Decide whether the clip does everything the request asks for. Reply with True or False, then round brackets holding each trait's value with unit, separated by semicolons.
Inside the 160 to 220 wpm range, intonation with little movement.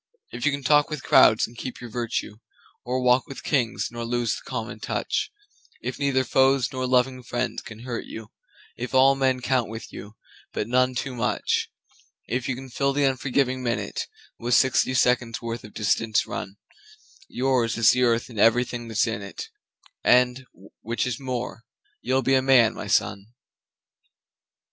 True (170 wpm; 2.1 semitones)